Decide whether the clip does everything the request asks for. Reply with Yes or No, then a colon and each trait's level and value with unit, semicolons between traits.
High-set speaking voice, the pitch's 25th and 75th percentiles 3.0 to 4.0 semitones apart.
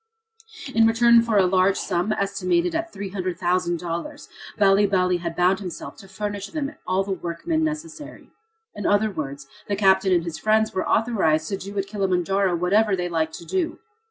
Yes: high, 195 Hz; average, 3.4 semitones